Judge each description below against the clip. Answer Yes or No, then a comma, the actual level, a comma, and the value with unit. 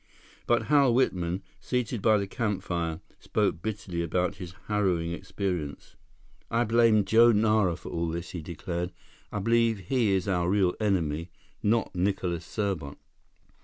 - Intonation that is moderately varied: Yes, average, 4.2 semitones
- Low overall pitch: Yes, very low, 95 Hz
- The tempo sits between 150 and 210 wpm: No, average, 140 wpm